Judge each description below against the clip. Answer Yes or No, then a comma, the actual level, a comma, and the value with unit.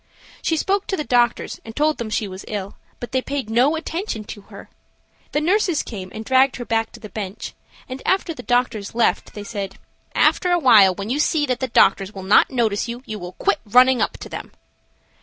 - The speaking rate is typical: No, fast, 215 wpm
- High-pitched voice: Yes, high, 240 Hz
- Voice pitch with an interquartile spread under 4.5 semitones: No, average, 5.2 semitones